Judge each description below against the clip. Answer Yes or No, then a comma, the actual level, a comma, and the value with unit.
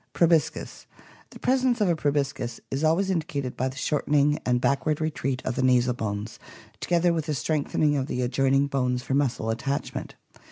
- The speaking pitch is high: No, medium, 140 Hz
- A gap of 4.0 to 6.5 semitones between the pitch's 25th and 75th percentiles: No, average, 3.6 semitones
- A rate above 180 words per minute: No, average, 175 wpm